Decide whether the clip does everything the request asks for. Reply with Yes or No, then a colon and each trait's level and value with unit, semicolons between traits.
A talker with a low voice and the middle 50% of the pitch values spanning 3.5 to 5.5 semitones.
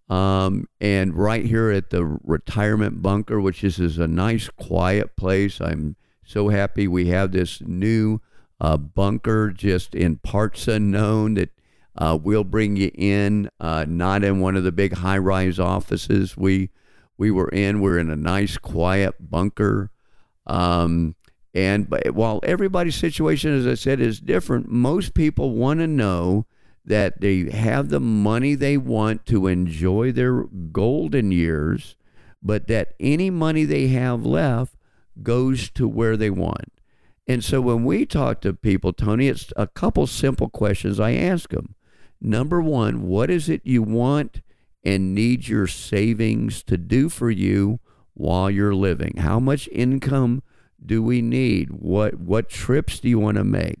Yes: low, 105 Hz; average, 3.9 semitones